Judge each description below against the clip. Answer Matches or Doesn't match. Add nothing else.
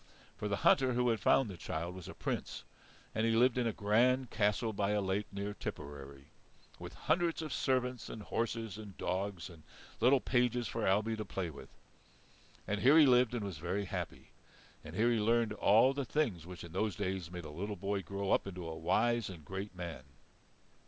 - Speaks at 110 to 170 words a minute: Doesn't match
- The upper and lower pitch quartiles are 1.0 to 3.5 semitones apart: Doesn't match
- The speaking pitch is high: Doesn't match